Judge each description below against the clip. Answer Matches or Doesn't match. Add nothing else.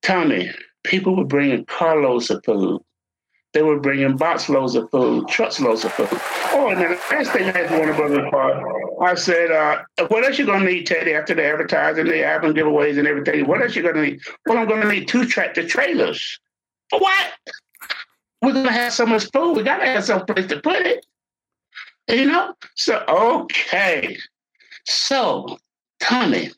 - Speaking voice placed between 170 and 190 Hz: Matches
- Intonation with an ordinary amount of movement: Doesn't match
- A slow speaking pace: Doesn't match